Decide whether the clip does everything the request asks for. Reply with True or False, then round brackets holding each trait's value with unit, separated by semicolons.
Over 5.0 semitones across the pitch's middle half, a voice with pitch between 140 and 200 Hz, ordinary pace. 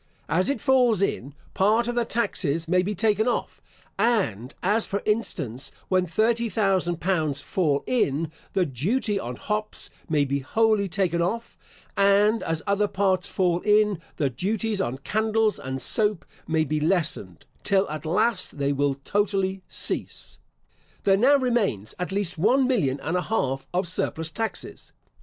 True (5.5 semitones; 190 Hz; 155 wpm)